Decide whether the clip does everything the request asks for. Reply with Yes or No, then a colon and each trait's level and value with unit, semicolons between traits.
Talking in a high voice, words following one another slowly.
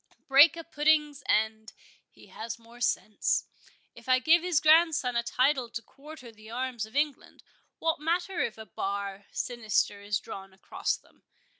No: very high, 250 Hz; average, 155 wpm